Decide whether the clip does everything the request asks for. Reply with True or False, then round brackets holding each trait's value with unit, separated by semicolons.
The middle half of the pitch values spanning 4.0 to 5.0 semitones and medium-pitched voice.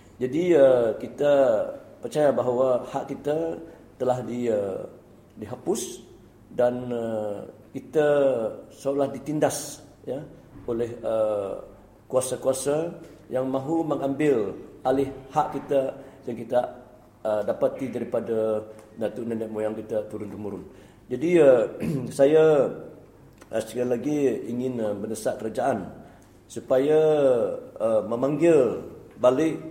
False (4.3 semitones; 130 Hz)